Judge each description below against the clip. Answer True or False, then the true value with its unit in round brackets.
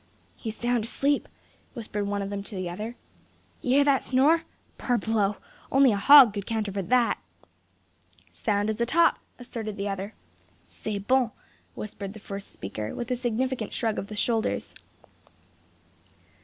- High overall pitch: True (220 Hz)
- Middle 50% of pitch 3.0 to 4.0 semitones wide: True (3.6 semitones)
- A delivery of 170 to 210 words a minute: False (150 wpm)